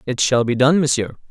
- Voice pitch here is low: Yes, low, 130 Hz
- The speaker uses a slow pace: No, fast, 230 wpm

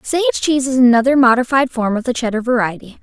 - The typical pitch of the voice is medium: No, very high, 250 Hz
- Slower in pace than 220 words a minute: Yes, average, 200 wpm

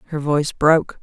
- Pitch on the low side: No, medium, 150 Hz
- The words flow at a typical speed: Yes, average, 175 wpm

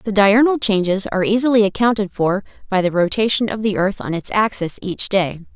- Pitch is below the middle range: No, high, 205 Hz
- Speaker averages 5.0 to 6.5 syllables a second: Yes, 5.5 syllables/s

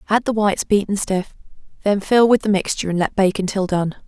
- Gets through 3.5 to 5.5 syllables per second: No, 5.9 syllables/s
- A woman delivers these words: Yes, female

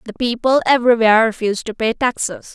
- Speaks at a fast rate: No, average, 165 wpm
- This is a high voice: Yes, high, 230 Hz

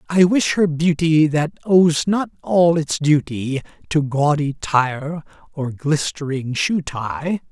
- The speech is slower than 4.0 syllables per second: Yes, 3.2 syllables/s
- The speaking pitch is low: No, medium, 155 Hz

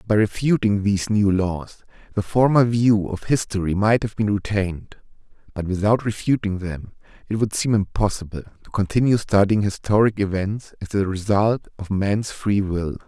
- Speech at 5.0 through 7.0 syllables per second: No, 4.8 syllables/s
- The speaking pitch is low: Yes, low, 105 Hz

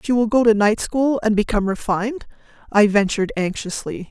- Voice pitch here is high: Yes, high, 215 Hz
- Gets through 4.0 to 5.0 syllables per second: No, 5.6 syllables/s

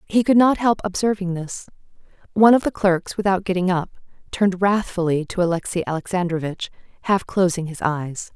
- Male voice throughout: No, female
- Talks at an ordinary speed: Yes, average, 160 wpm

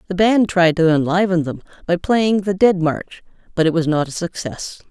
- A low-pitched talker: No, medium, 175 Hz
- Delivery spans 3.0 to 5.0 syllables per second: Yes, 4.9 syllables/s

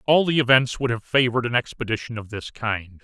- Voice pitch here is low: Yes, low, 120 Hz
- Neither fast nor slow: No, fast, 220 wpm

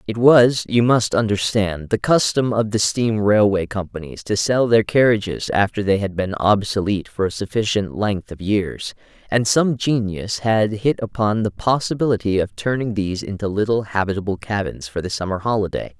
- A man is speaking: Yes, male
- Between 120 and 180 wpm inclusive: Yes, average, 175 wpm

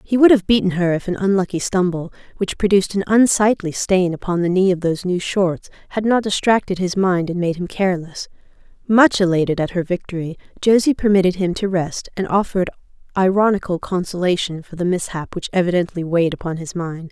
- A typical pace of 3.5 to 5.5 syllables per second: No, 5.8 syllables/s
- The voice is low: No, medium, 185 Hz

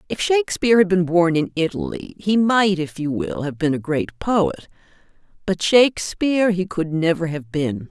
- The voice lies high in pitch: No, medium, 180 Hz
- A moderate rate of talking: Yes, average, 180 wpm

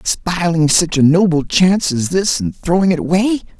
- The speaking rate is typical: Yes, average, 185 wpm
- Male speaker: Yes, male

